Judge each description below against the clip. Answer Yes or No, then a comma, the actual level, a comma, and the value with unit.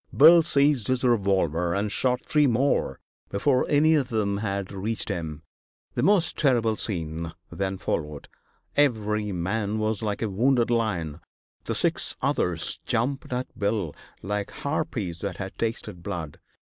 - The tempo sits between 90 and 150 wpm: Yes, average, 145 wpm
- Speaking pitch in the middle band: No, low, 105 Hz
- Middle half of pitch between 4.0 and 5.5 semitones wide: Yes, average, 5.0 semitones